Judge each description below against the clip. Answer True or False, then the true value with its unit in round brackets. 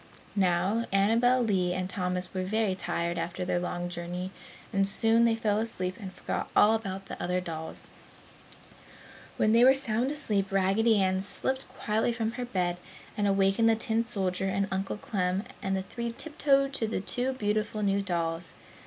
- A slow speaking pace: False (170 wpm)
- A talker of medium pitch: False (195 Hz)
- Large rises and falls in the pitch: False (3.6 semitones)